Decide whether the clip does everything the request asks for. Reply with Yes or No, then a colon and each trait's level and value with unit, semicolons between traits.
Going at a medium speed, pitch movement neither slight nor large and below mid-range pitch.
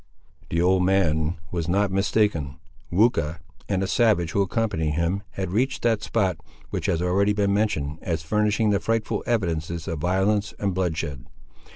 Yes: average, 160 wpm; average, 3.9 semitones; very low, 95 Hz